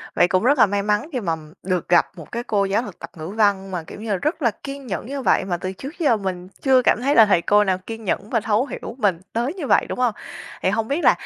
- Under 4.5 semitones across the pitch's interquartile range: No, average, 4.8 semitones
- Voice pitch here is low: No, high, 210 Hz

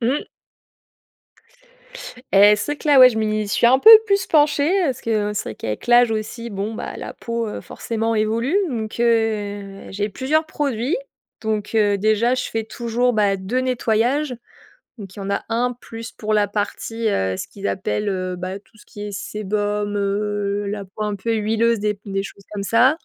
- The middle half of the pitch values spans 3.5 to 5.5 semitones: No, average, 2.7 semitones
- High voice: Yes, high, 215 Hz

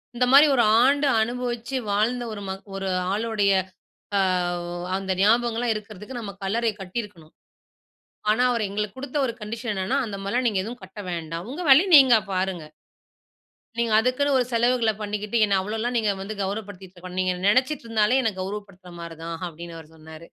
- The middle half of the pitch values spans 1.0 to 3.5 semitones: No, average, 3.9 semitones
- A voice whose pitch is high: Yes, high, 215 Hz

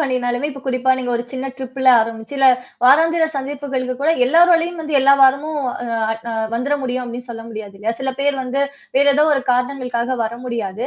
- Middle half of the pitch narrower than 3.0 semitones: Yes, narrow, 2.5 semitones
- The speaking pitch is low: No, very high, 260 Hz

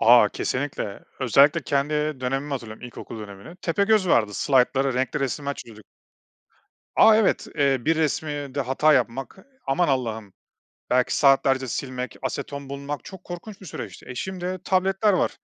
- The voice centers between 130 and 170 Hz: Yes, medium, 140 Hz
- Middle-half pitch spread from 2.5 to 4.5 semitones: Yes, average, 3.9 semitones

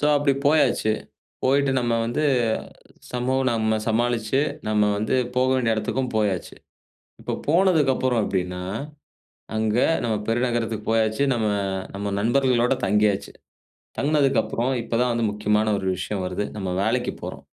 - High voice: No, low, 115 Hz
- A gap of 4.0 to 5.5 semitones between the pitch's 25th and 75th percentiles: No, average, 3.4 semitones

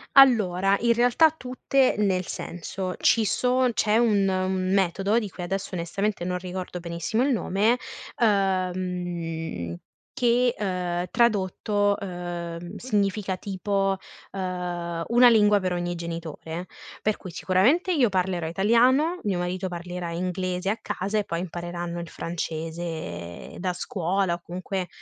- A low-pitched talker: No, medium, 185 Hz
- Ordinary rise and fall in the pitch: Yes, average, 3.2 semitones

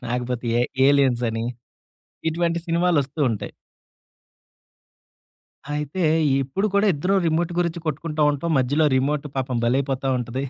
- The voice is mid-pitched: Yes, medium, 145 Hz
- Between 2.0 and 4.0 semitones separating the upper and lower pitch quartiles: No, average, 4.4 semitones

